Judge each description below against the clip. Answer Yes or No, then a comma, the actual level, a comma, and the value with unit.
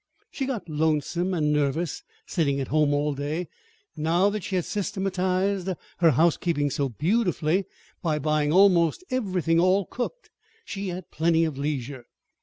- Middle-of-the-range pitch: Yes, medium, 170 Hz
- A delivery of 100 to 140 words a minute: No, average, 150 wpm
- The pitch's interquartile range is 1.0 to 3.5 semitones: No, average, 4.0 semitones